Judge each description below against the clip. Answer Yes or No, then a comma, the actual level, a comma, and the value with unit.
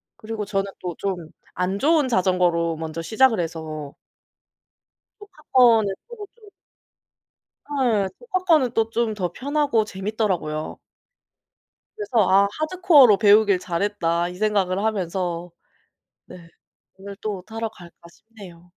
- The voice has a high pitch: Yes, high, 205 Hz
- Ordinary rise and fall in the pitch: Yes, average, 4.7 semitones